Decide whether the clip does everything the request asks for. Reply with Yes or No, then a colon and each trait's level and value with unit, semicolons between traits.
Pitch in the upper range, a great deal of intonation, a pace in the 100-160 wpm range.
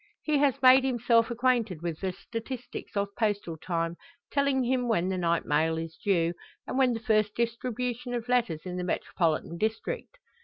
No: high, 225 Hz; wide, 6.2 semitones; average, 175 wpm